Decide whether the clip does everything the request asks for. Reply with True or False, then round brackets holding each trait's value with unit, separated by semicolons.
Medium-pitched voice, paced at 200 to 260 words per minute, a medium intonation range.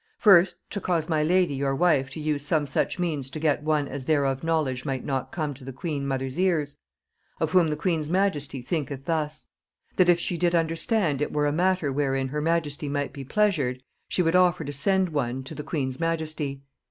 True (150 Hz; 205 wpm; 3.4 semitones)